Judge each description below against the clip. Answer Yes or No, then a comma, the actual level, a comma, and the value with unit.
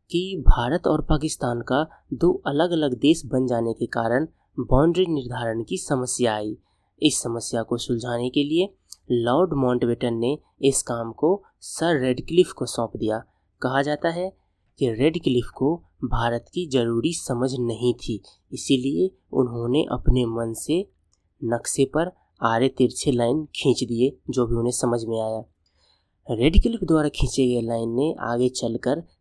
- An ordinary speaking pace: Yes, average, 150 wpm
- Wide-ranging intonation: No, average, 4.1 semitones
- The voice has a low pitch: Yes, low, 125 Hz